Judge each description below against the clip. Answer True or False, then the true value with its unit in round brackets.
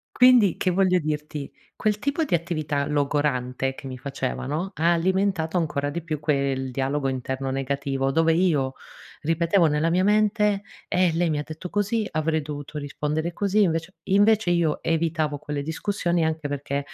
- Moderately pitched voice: True (160 Hz)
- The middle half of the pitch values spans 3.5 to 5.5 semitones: True (4.1 semitones)